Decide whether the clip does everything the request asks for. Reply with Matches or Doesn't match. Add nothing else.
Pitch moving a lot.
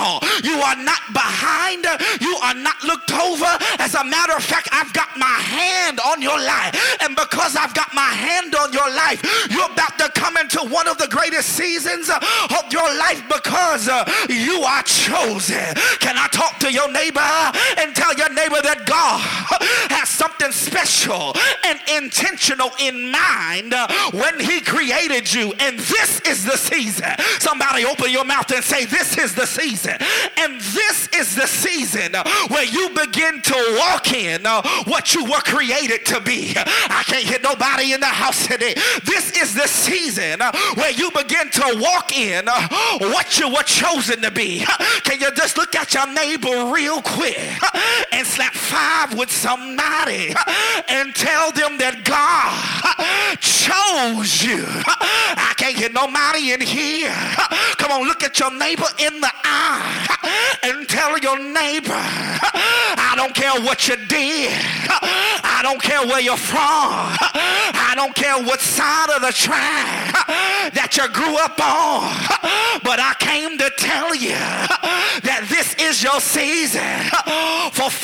Doesn't match